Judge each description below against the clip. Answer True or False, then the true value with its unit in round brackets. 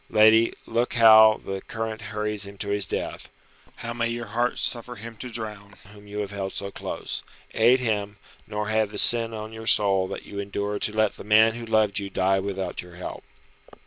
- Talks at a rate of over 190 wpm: True (205 wpm)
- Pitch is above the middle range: False (105 Hz)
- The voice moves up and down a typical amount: False (1.9 semitones)